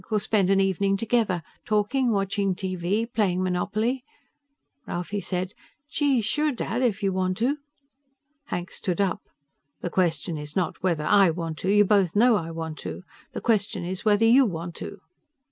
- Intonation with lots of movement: No, average, 3.5 semitones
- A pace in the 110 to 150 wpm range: No, average, 165 wpm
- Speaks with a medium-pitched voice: No, high, 195 Hz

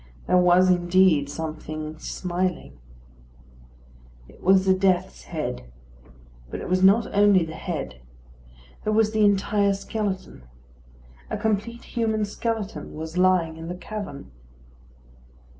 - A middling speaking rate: No, slow, 120 wpm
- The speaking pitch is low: No, medium, 185 Hz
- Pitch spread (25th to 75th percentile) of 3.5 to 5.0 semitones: Yes, average, 4.2 semitones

